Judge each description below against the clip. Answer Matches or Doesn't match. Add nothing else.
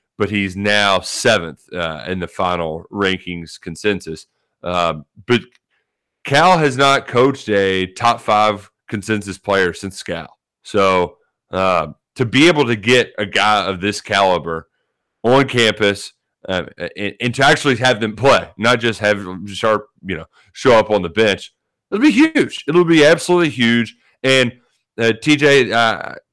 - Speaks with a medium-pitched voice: Doesn't match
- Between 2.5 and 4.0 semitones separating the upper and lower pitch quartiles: Doesn't match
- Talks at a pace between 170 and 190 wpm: Doesn't match